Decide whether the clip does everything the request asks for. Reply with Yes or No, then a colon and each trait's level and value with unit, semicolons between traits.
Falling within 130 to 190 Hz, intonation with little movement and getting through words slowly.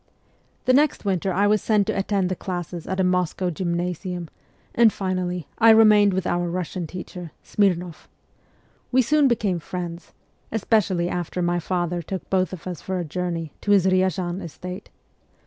No: medium, 185 Hz; narrow, 2.3 semitones; average, 165 wpm